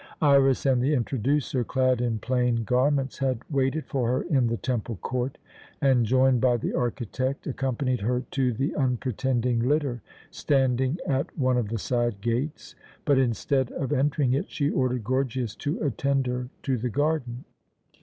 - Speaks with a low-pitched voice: Yes, low, 130 Hz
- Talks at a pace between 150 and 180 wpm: Yes, average, 160 wpm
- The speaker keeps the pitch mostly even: Yes, narrow, 2.1 semitones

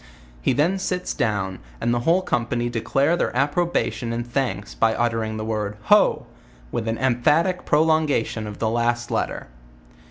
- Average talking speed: Yes, average, 160 wpm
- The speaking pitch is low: Yes, low, 120 Hz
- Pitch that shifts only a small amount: No, average, 5.0 semitones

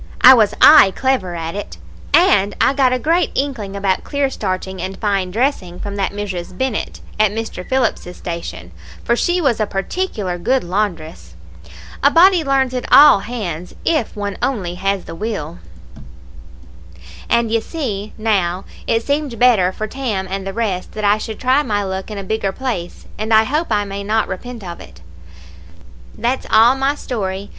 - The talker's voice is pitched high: Yes, high, 210 Hz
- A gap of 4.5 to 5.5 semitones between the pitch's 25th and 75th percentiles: Yes, average, 5.1 semitones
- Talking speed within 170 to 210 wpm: Yes, average, 175 wpm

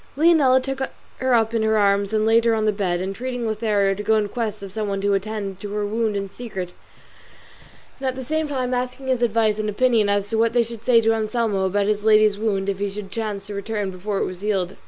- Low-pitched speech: No, high, 215 Hz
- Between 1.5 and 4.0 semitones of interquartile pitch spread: Yes, narrow, 2.5 semitones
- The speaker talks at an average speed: No, fast, 245 wpm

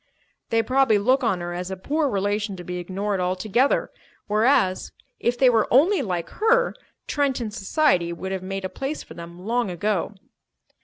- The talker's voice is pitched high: Yes, high, 210 Hz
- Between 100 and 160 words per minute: No, average, 170 wpm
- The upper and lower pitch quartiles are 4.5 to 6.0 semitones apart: Yes, wide, 5.6 semitones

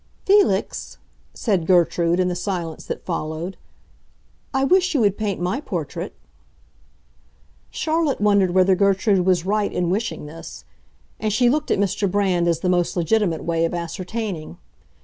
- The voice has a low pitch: No, high, 190 Hz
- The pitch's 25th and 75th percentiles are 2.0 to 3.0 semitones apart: No, average, 3.7 semitones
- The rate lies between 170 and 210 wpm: No, average, 150 wpm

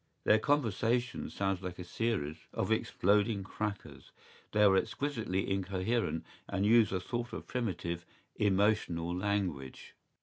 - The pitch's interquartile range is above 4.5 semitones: No, average, 3.5 semitones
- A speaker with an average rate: No, slow, 130 wpm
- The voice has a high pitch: No, low, 100 Hz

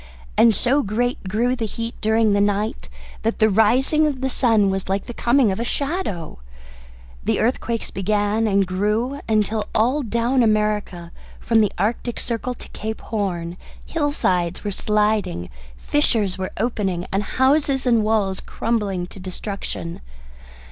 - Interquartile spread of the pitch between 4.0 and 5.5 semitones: No, average, 3.4 semitones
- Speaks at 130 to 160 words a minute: Yes, average, 150 wpm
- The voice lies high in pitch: Yes, high, 215 Hz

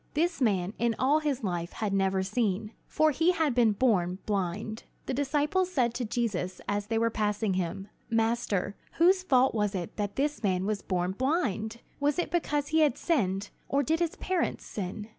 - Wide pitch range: Yes, wide, 6.6 semitones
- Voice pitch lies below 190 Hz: No, high, 225 Hz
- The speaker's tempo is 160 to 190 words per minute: Yes, average, 185 wpm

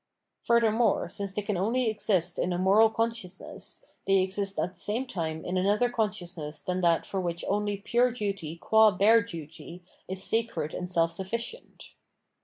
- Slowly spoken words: No, average, 165 wpm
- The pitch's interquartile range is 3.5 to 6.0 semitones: Yes, average, 3.8 semitones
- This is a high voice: Yes, high, 195 Hz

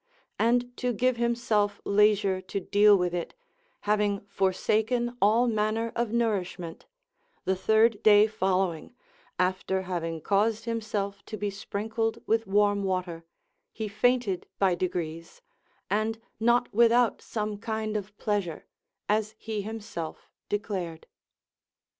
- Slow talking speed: Yes, slow, 120 wpm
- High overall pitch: Yes, high, 210 Hz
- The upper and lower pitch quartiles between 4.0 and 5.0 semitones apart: No, average, 2.8 semitones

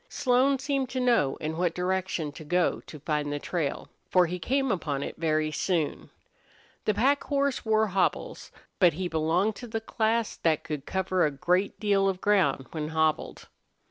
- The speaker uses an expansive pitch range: Yes, wide, 5.7 semitones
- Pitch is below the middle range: No, medium, 180 Hz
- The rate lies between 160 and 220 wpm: Yes, average, 175 wpm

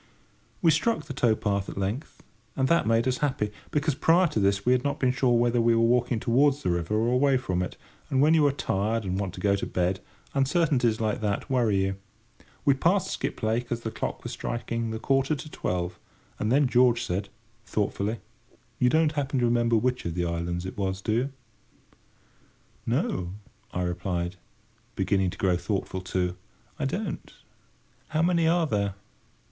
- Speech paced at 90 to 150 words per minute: No, average, 185 wpm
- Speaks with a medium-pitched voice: No, low, 115 Hz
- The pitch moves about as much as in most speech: No, wide, 5.7 semitones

